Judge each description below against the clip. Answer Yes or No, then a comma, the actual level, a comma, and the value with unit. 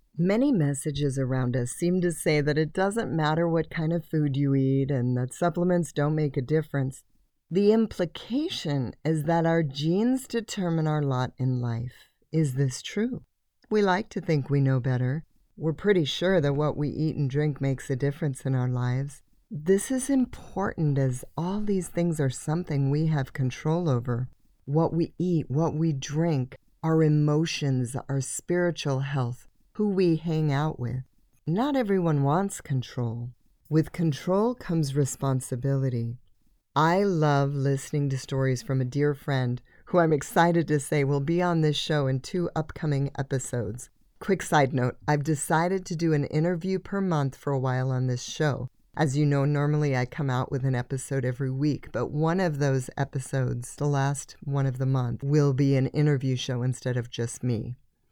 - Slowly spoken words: No, average, 175 wpm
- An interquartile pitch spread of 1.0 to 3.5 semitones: No, average, 3.9 semitones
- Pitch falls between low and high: Yes, medium, 145 Hz